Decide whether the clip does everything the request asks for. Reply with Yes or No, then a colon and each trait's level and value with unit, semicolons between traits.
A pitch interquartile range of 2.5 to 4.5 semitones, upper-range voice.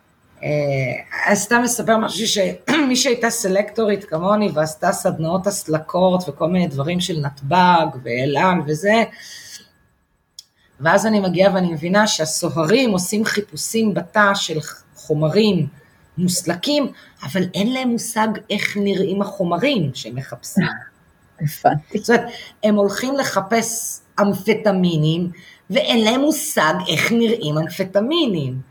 No: wide, 5.4 semitones; high, 195 Hz